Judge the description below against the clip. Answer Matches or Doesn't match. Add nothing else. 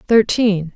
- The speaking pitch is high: Matches